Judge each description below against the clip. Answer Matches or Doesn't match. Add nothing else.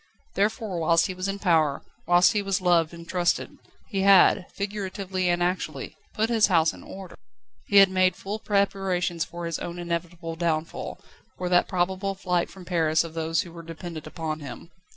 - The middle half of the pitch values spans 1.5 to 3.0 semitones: Matches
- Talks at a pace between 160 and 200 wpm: Matches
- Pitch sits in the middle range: Matches